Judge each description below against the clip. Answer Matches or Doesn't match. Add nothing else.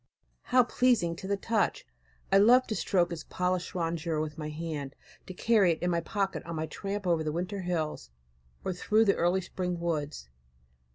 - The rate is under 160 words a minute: Doesn't match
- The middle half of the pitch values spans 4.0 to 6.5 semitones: Doesn't match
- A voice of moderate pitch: Matches